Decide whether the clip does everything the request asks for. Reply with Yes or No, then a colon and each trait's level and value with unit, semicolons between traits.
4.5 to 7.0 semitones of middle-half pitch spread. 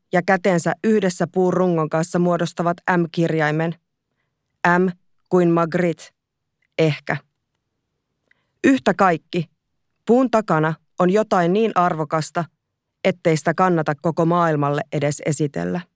No: narrow, 2.6 semitones